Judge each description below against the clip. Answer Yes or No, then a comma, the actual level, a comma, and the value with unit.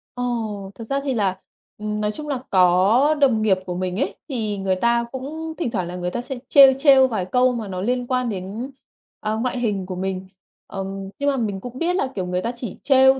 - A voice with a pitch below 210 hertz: No, high, 225 Hz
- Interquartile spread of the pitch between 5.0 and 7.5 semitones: Yes, average, 5.3 semitones